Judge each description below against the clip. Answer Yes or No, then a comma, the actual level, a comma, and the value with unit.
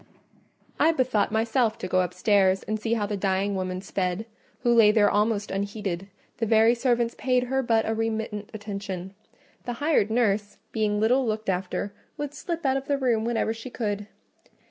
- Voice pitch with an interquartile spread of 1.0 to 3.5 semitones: Yes, average, 2.8 semitones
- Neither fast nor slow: Yes, average, 175 wpm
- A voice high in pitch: Yes, high, 220 Hz